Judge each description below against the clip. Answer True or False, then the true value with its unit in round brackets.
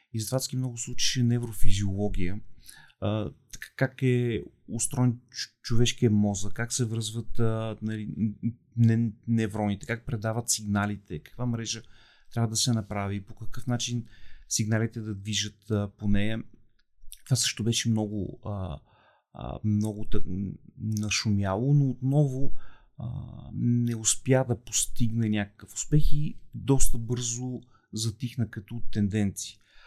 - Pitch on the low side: True (115 Hz)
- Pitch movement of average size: False (2.3 semitones)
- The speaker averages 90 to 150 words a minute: True (120 wpm)